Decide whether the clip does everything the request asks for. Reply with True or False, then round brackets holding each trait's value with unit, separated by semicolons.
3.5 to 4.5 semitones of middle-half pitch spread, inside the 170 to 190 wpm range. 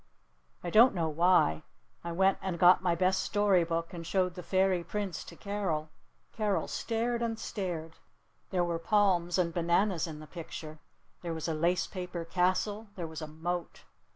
False (2.6 semitones; 175 wpm)